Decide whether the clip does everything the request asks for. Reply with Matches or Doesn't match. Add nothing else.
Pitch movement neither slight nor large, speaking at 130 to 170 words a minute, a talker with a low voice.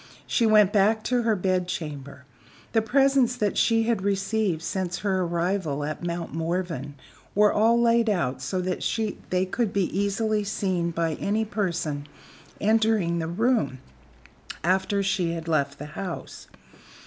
Doesn't match